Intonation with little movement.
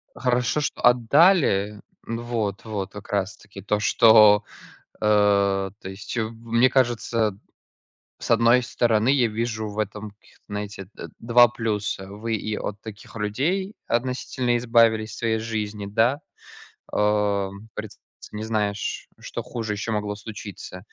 Yes: narrow, 2.2 semitones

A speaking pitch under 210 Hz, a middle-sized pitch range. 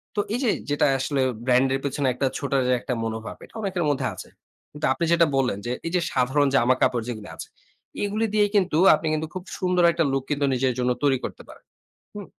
Yes: medium, 140 Hz; average, 5.0 semitones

